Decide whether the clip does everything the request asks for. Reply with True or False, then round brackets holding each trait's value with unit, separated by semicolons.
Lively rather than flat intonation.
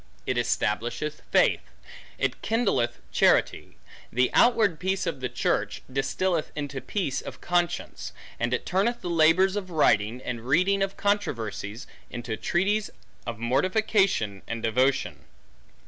True (8.1 semitones)